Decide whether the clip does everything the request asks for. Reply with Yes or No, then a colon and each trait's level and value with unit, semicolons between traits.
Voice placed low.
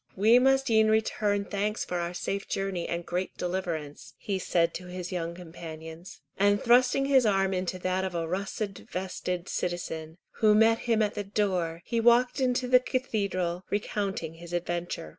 No: high, 190 Hz